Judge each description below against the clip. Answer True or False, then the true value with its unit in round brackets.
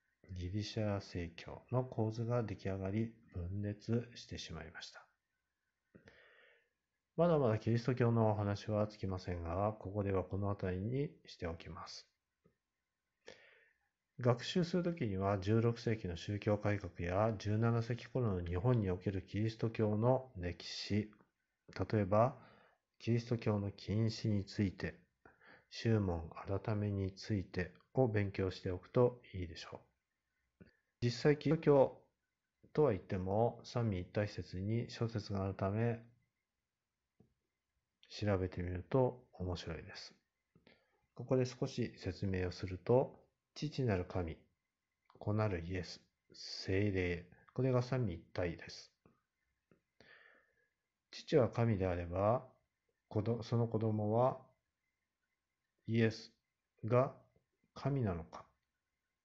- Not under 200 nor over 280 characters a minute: True (220 characters per minute)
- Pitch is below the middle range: True (105 Hz)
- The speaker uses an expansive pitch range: False (3.9 semitones)